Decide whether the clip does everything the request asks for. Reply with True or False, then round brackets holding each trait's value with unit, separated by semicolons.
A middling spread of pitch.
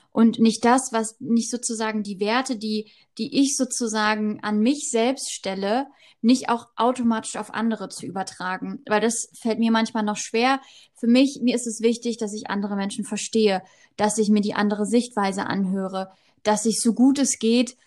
False (2.3 semitones)